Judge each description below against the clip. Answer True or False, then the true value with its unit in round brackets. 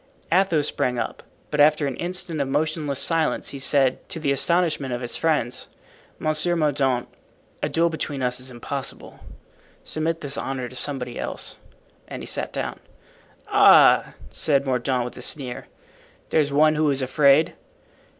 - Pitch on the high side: False (140 Hz)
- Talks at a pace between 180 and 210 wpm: False (155 wpm)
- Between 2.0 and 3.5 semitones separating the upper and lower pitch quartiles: True (3.1 semitones)